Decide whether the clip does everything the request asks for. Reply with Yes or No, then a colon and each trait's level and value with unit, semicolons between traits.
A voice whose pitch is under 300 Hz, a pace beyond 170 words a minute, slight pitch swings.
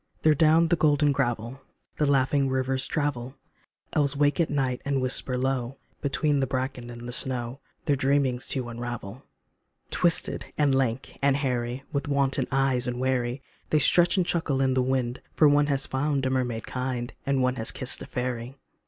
Yes: low, 135 Hz; average, 180 wpm; narrow, 2.1 semitones